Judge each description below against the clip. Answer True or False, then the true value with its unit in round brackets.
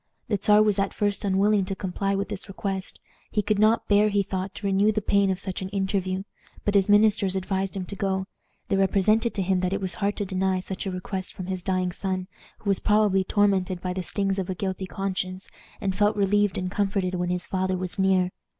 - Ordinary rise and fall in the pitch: False (1.5 semitones)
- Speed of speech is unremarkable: False (225 wpm)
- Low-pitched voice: False (195 Hz)